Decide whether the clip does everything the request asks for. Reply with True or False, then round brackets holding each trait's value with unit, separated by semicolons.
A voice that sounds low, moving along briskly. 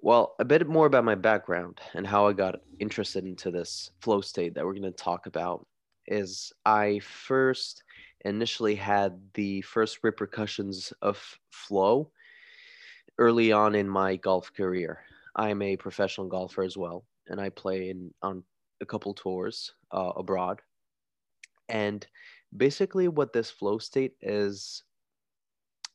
False (100 Hz; 145 wpm)